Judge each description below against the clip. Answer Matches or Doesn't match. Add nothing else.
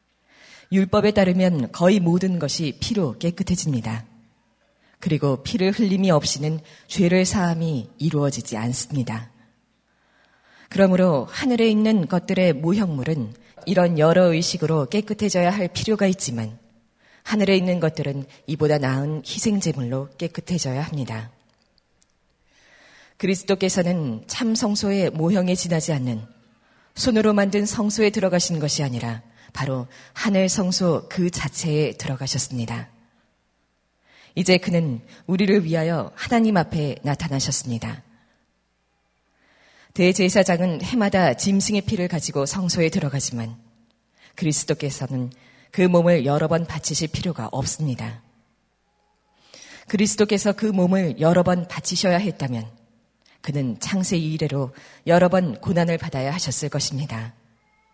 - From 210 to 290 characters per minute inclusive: Matches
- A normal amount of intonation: Doesn't match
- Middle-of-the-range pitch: Matches